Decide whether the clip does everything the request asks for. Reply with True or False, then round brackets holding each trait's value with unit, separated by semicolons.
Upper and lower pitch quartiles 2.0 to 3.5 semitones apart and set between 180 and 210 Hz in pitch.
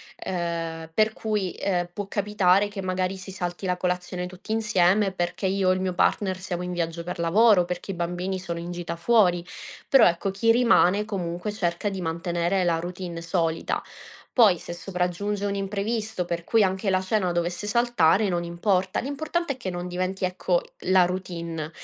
True (2.6 semitones; 185 Hz)